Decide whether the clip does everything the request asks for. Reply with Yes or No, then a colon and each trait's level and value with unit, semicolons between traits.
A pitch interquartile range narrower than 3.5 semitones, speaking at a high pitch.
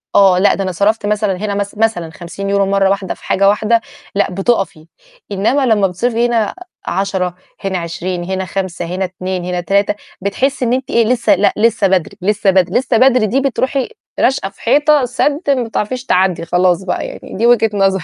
No: average, 3.9 semitones; high, 200 Hz